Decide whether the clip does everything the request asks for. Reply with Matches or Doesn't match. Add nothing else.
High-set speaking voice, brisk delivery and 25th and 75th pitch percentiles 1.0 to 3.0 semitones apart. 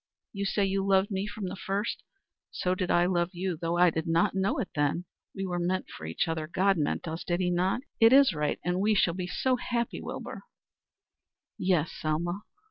Doesn't match